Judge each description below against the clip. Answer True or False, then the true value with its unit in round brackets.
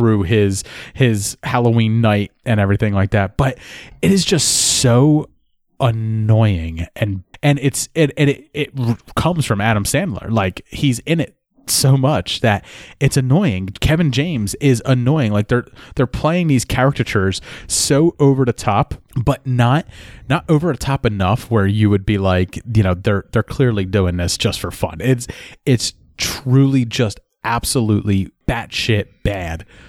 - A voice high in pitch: False (115 Hz)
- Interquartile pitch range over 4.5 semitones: True (5.2 semitones)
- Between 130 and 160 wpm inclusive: True (155 wpm)